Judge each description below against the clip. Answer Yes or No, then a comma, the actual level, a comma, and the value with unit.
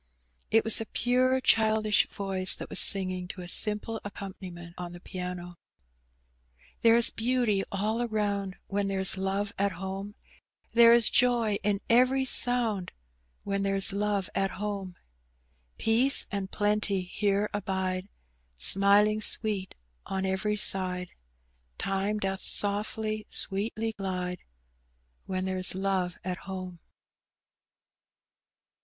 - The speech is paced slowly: Yes, slow, 120 wpm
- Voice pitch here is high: Yes, high, 200 Hz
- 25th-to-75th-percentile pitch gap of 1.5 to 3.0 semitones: Yes, narrow, 2.4 semitones